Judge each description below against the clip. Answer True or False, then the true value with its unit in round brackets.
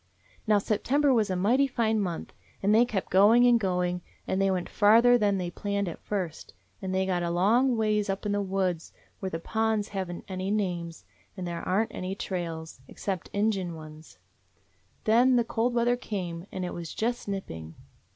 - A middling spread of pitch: True (3.6 semitones)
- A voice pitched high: True (195 Hz)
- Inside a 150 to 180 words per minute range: False (190 wpm)